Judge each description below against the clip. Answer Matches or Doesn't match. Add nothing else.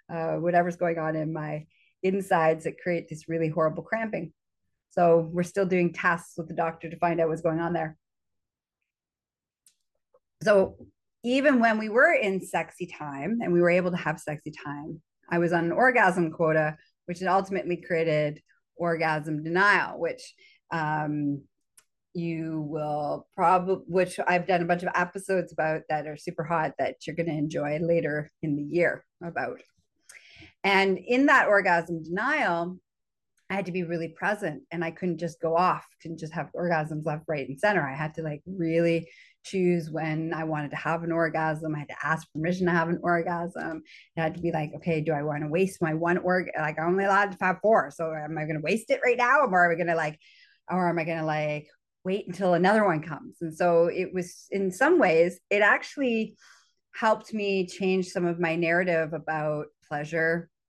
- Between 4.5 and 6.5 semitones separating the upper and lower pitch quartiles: Doesn't match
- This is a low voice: Doesn't match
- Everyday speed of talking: Matches